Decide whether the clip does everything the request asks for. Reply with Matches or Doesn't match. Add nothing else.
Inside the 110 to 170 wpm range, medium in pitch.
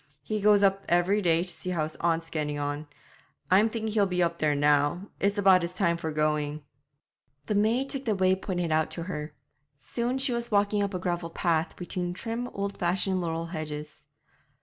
Doesn't match